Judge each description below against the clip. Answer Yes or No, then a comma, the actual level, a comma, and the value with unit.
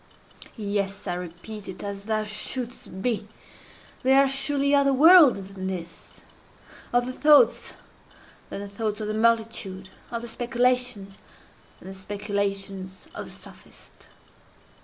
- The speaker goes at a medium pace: No, slow, 115 wpm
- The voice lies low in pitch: No, high, 210 Hz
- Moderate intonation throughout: Yes, average, 4.3 semitones